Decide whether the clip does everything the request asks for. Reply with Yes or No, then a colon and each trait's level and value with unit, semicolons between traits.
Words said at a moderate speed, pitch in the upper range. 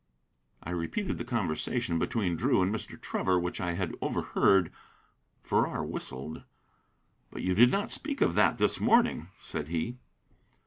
No: average, 145 wpm; very low, 90 Hz